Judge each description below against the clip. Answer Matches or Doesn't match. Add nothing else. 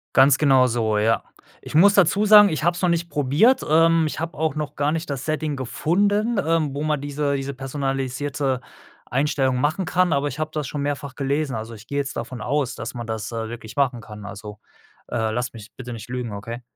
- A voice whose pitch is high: Doesn't match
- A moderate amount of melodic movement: Matches